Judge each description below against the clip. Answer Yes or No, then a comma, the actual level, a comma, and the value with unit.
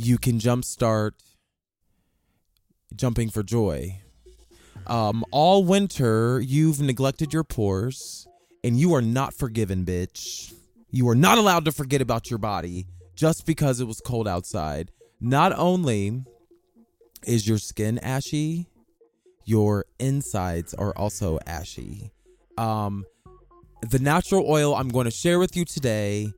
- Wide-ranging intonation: Yes, wide, 6.6 semitones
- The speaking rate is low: Yes, slow, 130 wpm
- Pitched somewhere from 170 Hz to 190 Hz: No, low, 120 Hz